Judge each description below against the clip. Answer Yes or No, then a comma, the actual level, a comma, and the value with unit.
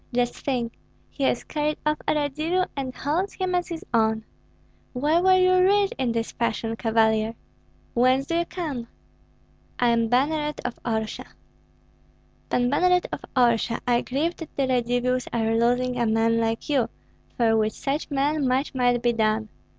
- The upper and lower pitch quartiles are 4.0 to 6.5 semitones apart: Yes, average, 4.6 semitones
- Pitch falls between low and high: No, very high, 250 Hz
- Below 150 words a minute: No, average, 165 wpm